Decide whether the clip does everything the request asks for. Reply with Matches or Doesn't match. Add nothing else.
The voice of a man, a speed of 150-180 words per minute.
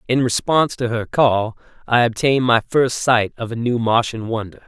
Doesn't match